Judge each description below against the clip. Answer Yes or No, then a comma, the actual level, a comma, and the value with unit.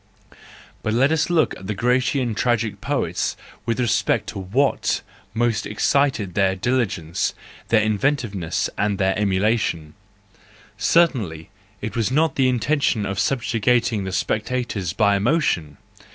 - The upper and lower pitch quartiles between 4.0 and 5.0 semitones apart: Yes, average, 4.5 semitones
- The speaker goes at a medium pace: No, slow, 125 wpm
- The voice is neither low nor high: No, low, 110 Hz